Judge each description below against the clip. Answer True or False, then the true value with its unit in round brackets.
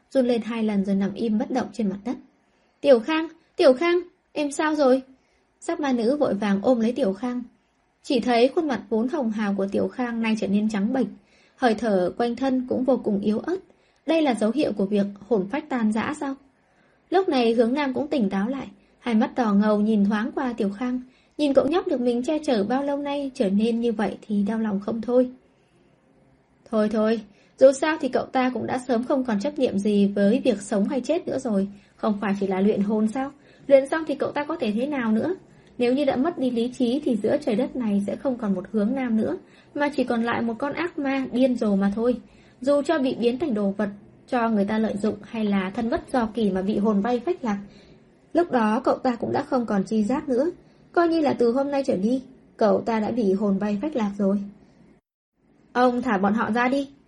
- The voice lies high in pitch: True (245 Hz)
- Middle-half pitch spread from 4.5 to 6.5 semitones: False (4.1 semitones)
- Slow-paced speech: False (240 wpm)